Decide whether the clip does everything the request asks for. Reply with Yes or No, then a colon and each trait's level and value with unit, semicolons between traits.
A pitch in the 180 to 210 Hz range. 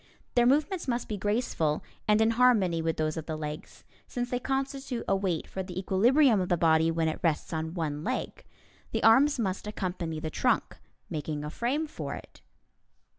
Yes: high, 190 Hz